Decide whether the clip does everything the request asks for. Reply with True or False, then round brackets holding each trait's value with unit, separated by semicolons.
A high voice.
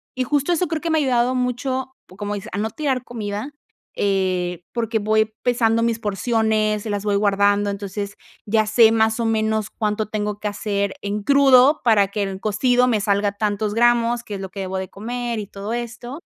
True (215 Hz)